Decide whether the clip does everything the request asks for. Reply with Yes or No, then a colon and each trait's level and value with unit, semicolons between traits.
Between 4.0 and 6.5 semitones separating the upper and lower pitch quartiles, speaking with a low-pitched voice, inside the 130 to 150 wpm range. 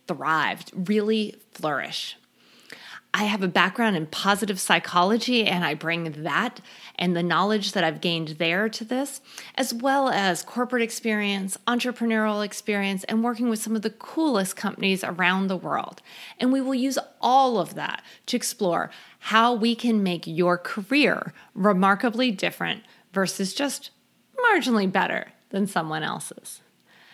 No: average, 4.6 semitones; high, 210 Hz; average, 145 wpm